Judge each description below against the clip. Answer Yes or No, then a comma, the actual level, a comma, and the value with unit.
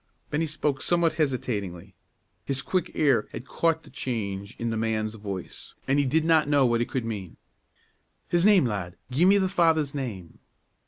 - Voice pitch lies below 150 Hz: Yes, low, 135 Hz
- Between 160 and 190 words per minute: Yes, average, 175 wpm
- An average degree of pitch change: No, wide, 6.7 semitones